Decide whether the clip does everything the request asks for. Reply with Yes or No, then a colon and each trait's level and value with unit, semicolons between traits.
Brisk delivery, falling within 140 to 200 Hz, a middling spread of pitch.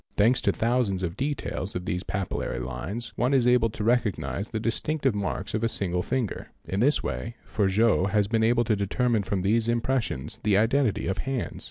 No: fast, 210 wpm; low, 110 Hz; average, 3.8 semitones